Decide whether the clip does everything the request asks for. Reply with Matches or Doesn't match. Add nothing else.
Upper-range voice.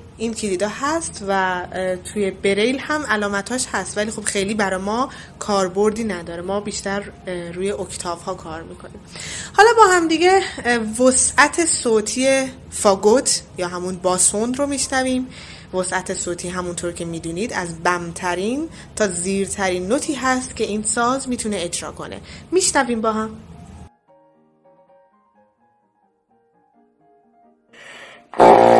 Matches